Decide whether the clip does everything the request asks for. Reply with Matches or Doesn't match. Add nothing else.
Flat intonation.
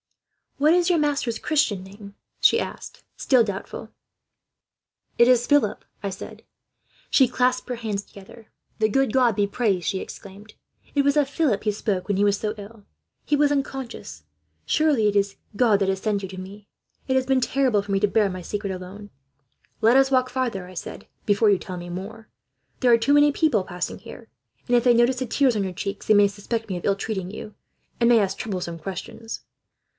Doesn't match